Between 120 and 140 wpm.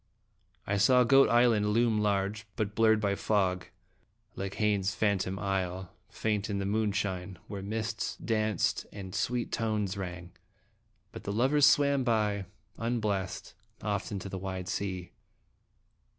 Yes: slow, 135 wpm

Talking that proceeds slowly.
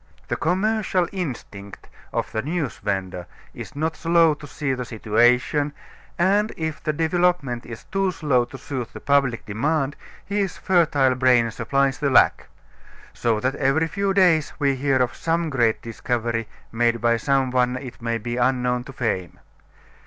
No: average, 160 wpm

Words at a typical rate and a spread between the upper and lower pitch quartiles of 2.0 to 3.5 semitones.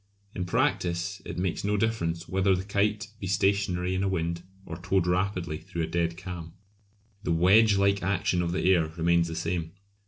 Yes: average, 185 wpm; narrow, 2.6 semitones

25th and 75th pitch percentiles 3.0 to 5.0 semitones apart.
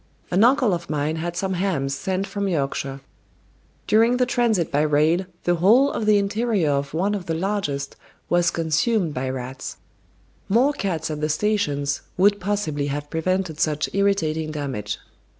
No: wide, 5.4 semitones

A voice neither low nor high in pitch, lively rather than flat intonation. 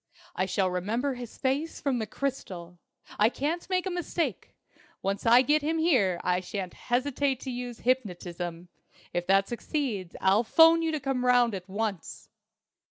No: high, 240 Hz; wide, 6.7 semitones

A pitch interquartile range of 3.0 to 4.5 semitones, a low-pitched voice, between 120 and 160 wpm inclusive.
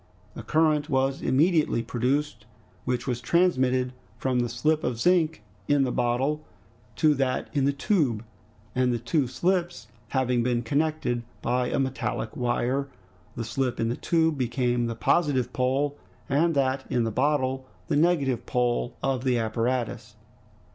Yes: average, 3.3 semitones; low, 130 Hz; average, 150 wpm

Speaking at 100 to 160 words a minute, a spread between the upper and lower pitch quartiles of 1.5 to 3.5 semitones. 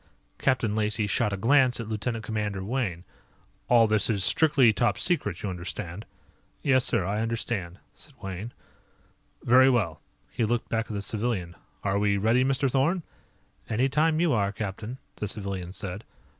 No: average, 155 wpm; average, 4.0 semitones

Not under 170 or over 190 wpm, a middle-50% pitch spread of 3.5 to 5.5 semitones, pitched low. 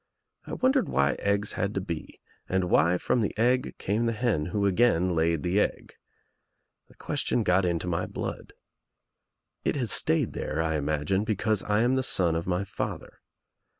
Yes: average, 175 wpm; average, 4.6 semitones; very low, 95 Hz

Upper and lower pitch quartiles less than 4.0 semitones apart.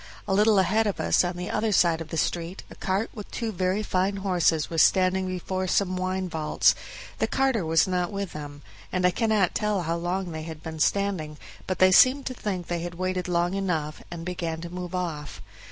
Yes: narrow, 2.5 semitones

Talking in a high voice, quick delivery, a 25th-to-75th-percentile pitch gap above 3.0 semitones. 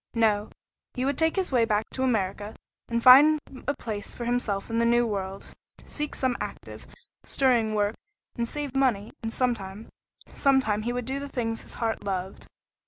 No: high, 235 Hz; average, 175 wpm; average, 3.8 semitones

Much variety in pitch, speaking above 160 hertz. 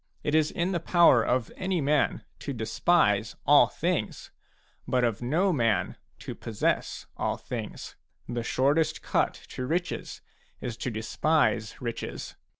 No: wide, 5.7 semitones; low, 135 Hz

